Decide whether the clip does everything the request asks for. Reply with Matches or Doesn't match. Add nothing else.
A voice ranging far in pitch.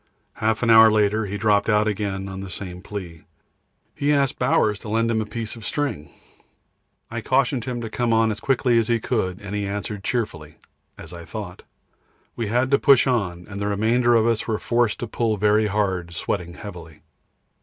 Doesn't match